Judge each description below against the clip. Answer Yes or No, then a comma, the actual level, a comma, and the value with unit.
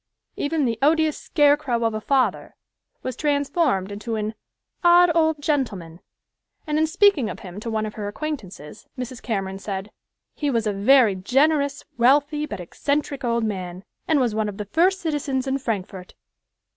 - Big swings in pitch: Yes, wide, 6.1 semitones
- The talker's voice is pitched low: No, very high, 255 Hz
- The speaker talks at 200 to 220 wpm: No, average, 165 wpm